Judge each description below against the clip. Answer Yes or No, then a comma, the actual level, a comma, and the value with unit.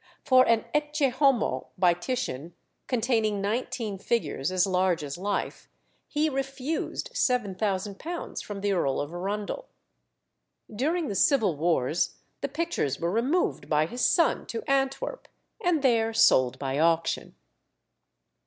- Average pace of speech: No, slow, 125 wpm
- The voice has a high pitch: Yes, high, 215 Hz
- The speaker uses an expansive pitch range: Yes, wide, 7.5 semitones